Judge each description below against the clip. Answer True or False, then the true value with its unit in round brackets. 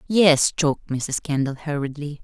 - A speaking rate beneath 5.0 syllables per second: True (4.6 syllables/s)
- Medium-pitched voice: True (150 Hz)